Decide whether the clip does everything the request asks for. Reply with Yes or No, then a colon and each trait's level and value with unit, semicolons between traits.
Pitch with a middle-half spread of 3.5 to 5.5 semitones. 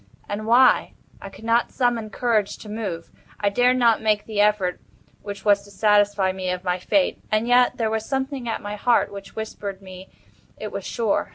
No: average, 2.7 semitones